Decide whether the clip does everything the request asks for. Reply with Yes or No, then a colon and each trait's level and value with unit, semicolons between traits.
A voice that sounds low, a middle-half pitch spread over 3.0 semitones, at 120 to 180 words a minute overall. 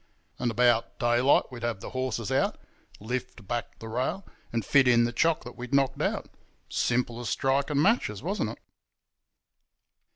No: low, 125 Hz; narrow, 2.4 semitones; average, 160 wpm